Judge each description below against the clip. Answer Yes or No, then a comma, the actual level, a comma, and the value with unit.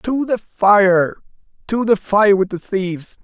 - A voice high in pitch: Yes, high, 200 Hz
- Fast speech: No, average, 165 wpm